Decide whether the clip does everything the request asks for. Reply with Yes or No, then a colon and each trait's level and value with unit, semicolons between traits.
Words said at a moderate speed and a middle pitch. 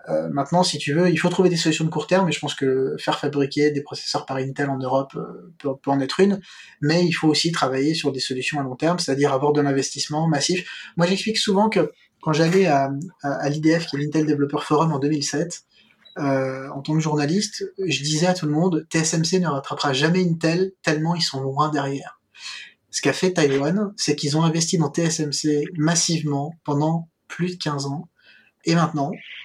Yes: average, 210 wpm; medium, 155 Hz